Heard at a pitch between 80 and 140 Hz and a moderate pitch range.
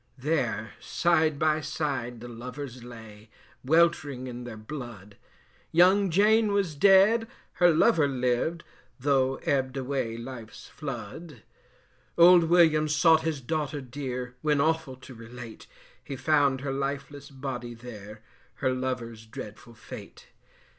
Yes: low, 135 Hz; average, 4.5 semitones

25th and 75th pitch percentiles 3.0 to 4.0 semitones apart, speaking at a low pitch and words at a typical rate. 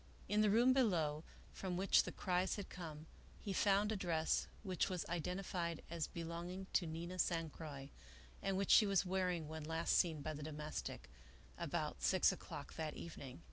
No: average, 3.3 semitones; medium, 175 Hz; average, 180 wpm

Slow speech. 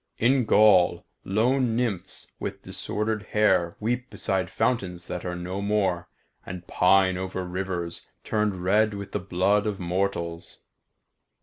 Yes: slow, 130 wpm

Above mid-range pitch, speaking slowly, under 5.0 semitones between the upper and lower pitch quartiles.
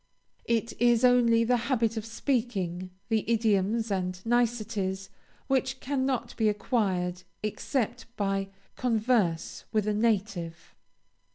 Yes: high, 225 Hz; slow, 110 wpm; average, 3.5 semitones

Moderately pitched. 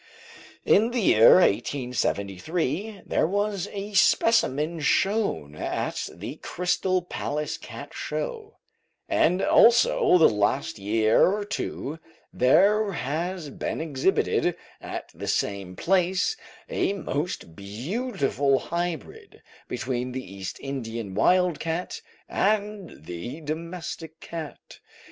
Yes: medium, 165 Hz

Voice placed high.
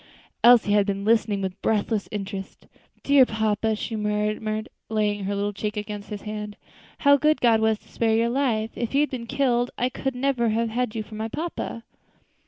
Yes: high, 220 Hz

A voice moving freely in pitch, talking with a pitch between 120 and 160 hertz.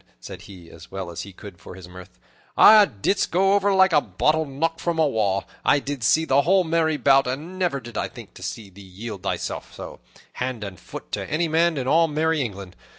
Yes: wide, 8.7 semitones; medium, 140 Hz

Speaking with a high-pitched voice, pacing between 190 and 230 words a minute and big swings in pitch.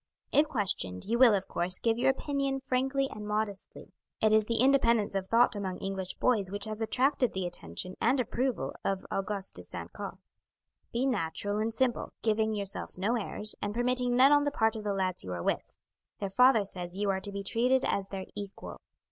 No: high, 215 Hz; average, 200 wpm; average, 4.2 semitones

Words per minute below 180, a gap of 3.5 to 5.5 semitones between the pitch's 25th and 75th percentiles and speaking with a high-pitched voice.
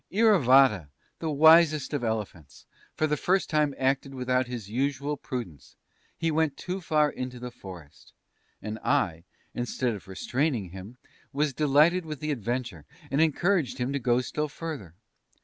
No: average, 150 wpm; average, 4.5 semitones; low, 135 Hz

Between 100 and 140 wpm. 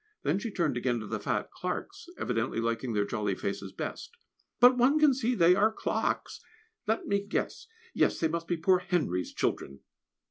No: average, 180 wpm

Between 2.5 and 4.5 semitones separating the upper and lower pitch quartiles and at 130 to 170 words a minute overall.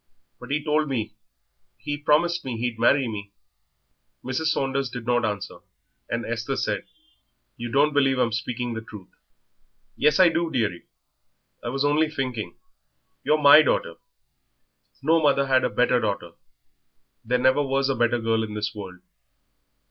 Yes: average, 4.2 semitones; average, 155 wpm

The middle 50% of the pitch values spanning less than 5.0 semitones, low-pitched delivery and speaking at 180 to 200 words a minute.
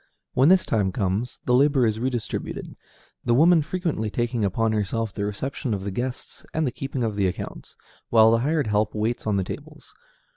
Yes: average, 4.0 semitones; low, 115 Hz; average, 190 wpm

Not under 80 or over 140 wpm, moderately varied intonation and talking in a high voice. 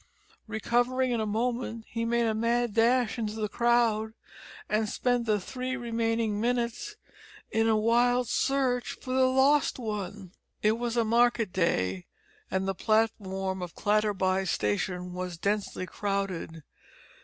Yes: slow, 135 wpm; average, 3.3 semitones; high, 225 Hz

